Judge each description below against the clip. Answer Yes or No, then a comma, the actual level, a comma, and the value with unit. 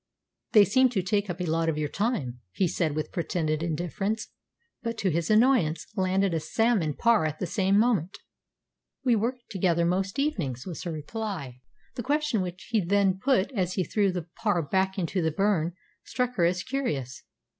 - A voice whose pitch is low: No, high, 190 Hz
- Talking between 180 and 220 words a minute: Yes, average, 185 wpm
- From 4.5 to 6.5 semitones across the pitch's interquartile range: Yes, average, 4.9 semitones